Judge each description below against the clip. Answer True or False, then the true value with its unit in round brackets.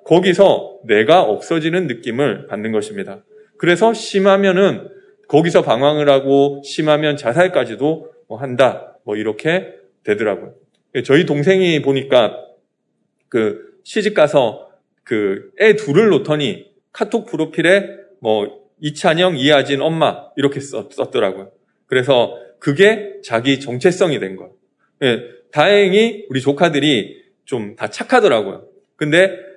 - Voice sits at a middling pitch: True (170 Hz)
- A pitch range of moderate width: False (6.1 semitones)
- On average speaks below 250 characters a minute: False (265 characters per minute)